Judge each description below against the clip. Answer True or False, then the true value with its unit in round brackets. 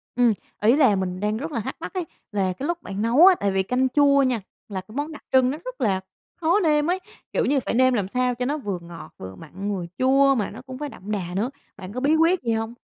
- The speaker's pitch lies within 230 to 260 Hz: True (250 Hz)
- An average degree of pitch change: False (6.1 semitones)